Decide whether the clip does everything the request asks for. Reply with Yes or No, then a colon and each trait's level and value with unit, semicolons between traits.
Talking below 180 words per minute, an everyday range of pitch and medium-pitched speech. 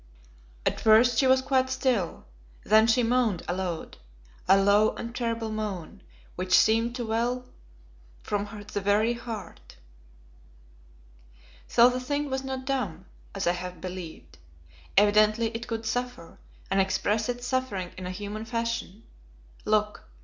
No: slow, 135 wpm; average, 3.7 semitones; high, 220 Hz